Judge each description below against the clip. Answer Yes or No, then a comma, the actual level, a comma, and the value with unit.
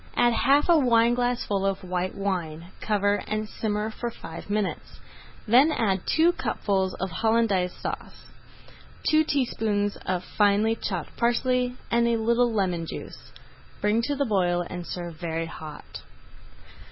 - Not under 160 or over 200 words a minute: No, average, 140 wpm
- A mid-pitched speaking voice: No, high, 210 Hz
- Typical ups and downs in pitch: Yes, average, 4.2 semitones